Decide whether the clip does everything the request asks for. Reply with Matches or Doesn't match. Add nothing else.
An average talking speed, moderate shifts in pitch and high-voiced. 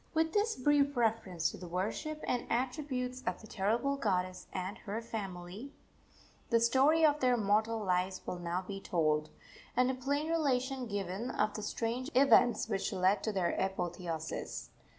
Doesn't match